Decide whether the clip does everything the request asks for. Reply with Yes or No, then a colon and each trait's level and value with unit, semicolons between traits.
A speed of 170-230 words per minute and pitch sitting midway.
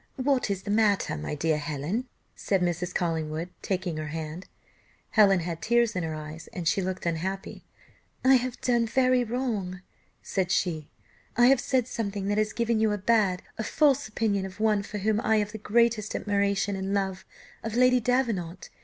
No: average, 180 wpm; high, 200 Hz